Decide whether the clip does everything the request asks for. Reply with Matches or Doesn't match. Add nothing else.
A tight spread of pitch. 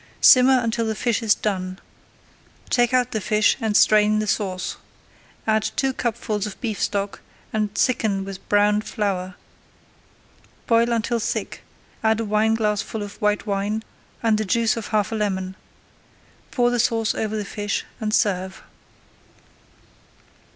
Matches